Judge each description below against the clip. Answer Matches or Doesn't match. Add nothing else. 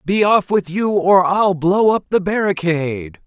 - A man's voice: Matches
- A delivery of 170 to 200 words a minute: Matches